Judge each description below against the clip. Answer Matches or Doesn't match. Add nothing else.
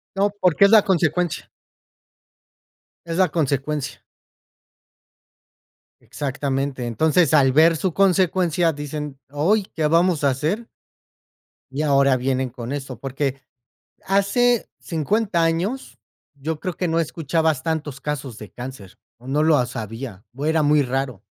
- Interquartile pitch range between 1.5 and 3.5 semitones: Doesn't match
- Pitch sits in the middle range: Matches